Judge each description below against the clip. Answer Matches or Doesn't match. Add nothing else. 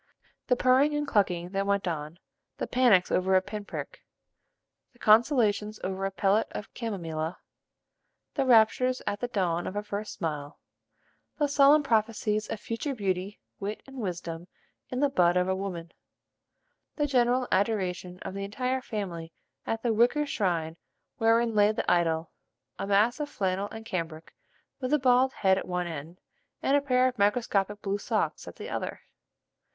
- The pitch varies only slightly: Doesn't match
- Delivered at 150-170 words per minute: Matches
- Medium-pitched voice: Doesn't match